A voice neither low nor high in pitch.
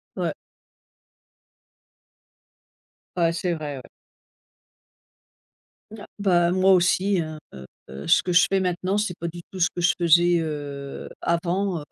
Yes: medium, 175 Hz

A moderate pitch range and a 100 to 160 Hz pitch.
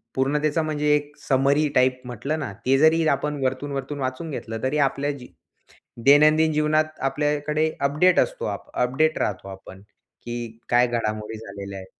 Yes: average, 3.6 semitones; medium, 140 Hz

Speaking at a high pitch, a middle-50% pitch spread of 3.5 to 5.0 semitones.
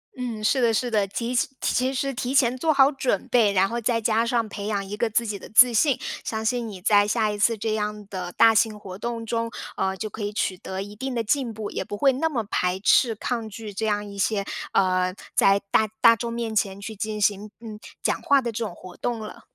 No: high, 220 Hz; narrow, 2.6 semitones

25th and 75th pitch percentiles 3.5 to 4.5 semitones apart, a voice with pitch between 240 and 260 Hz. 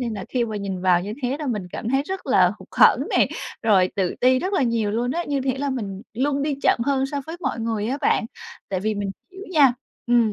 No: average, 5.1 semitones; high, 245 Hz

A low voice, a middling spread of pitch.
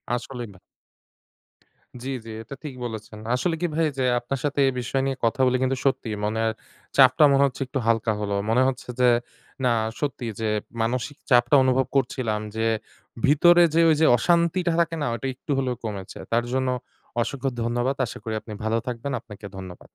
Yes: low, 130 Hz; average, 3.3 semitones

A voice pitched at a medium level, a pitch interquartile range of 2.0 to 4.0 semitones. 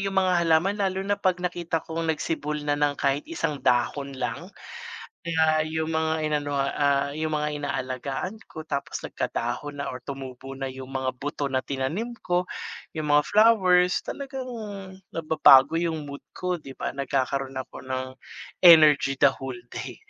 Yes: medium, 150 Hz; average, 3.5 semitones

